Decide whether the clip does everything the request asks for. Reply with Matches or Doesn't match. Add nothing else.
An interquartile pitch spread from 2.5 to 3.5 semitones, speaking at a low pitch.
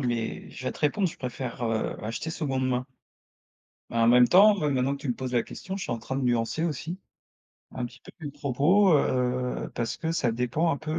Doesn't match